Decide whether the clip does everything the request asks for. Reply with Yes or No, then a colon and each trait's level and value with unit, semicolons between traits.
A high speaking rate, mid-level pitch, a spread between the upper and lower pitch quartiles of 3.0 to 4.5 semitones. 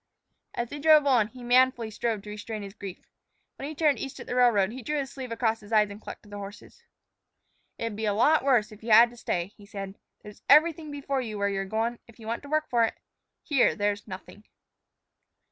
No: fast, 230 wpm; high, 230 Hz; average, 4.1 semitones